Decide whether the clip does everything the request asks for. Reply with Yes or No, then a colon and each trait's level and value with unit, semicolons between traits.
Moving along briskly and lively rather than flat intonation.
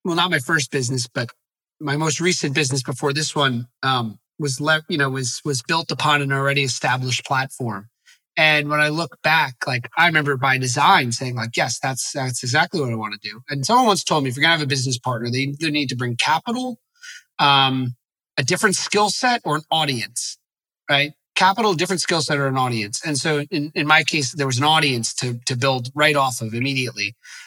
No: fast, 215 wpm; average, 3.7 semitones